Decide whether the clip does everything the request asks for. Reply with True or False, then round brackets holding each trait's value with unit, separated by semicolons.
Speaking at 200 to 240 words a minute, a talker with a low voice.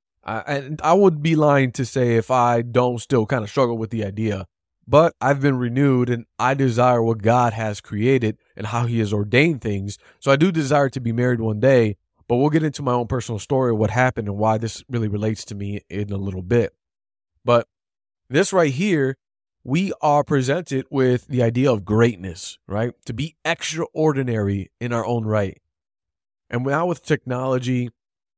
False (190 wpm; 120 Hz)